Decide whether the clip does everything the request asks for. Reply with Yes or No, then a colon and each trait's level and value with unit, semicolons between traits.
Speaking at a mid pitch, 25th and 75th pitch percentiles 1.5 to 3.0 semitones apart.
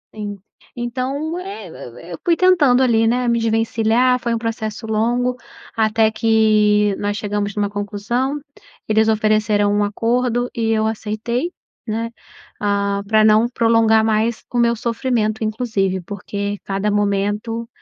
No: high, 220 Hz; narrow, 2.4 semitones